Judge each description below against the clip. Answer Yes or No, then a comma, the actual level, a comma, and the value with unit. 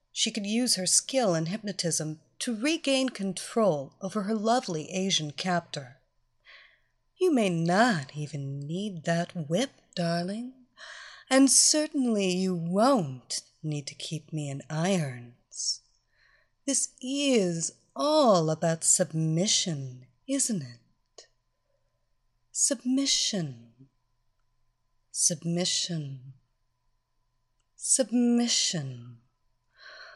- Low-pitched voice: No, medium, 170 Hz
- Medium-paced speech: No, slow, 85 wpm